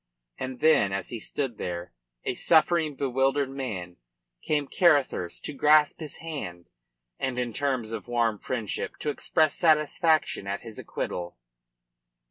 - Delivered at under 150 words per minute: Yes, slow, 135 wpm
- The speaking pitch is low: Yes, low, 130 Hz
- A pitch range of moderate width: No, wide, 5.7 semitones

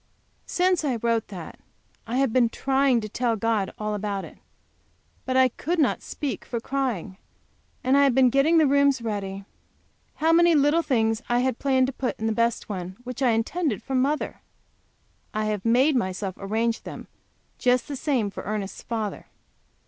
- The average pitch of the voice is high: Yes, high, 245 Hz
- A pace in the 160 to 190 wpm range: Yes, average, 180 wpm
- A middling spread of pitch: Yes, average, 4.2 semitones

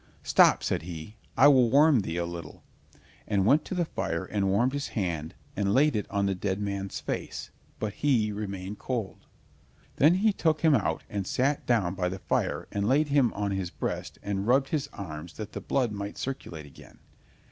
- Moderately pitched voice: No, low, 105 Hz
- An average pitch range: No, wide, 6.0 semitones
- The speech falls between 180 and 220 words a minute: Yes, average, 195 wpm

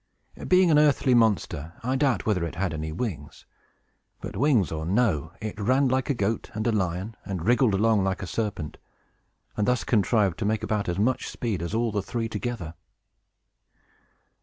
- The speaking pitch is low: Yes, low, 105 Hz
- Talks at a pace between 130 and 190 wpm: Yes, average, 180 wpm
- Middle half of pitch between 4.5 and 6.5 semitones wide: Yes, average, 5.0 semitones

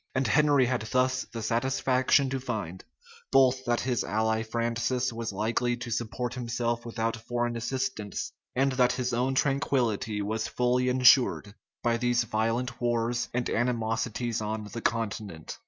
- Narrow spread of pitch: Yes, narrow, 2.1 semitones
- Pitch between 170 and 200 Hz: No, low, 120 Hz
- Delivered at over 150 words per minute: No, average, 145 wpm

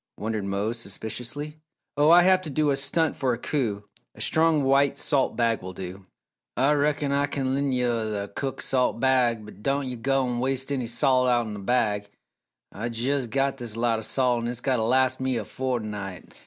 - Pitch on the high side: No, low, 125 Hz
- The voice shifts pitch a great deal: No, average, 3.6 semitones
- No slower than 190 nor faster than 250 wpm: Yes, average, 200 wpm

